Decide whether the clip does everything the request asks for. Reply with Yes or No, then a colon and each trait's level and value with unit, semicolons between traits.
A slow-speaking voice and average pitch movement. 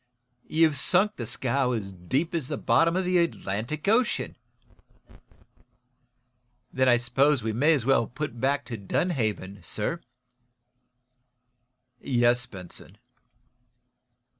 No: slow, 115 wpm; wide, 6.0 semitones